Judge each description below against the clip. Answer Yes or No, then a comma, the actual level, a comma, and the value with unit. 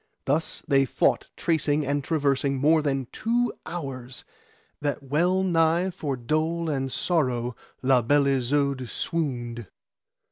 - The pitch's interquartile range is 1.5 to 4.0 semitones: Yes, average, 3.6 semitones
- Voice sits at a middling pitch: Yes, medium, 145 Hz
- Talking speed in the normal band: No, slow, 120 wpm